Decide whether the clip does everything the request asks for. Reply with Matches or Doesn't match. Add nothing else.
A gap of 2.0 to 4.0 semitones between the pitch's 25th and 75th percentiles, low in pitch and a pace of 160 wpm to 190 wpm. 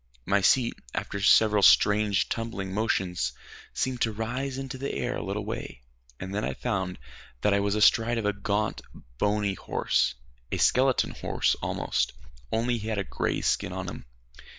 Matches